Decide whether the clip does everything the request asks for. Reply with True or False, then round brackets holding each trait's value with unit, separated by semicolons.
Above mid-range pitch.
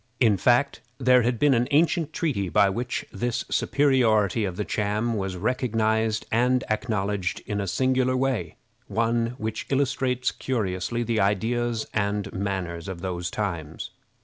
False (110 Hz)